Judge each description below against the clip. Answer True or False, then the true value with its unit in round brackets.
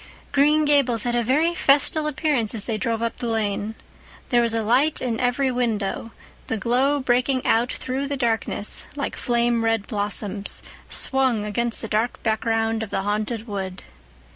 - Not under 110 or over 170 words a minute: True (165 wpm)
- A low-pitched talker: False (235 Hz)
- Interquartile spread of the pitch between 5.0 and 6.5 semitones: False (3.1 semitones)